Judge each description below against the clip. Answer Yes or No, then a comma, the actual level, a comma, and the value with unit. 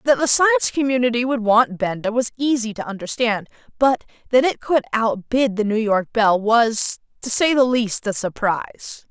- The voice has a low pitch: No, high, 230 Hz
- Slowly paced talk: No, average, 180 wpm